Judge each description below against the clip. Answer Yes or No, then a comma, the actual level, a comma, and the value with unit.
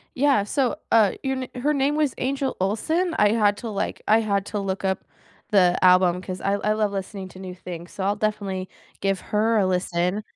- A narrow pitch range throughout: No, average, 3.3 semitones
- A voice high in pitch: Yes, high, 205 Hz